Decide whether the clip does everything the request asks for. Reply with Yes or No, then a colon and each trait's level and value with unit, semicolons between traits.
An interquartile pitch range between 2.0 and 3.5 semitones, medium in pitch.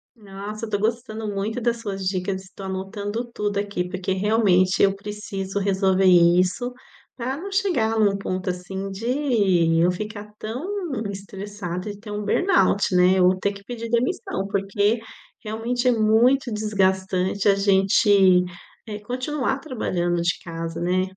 No: average, 3.0 semitones; high, 200 Hz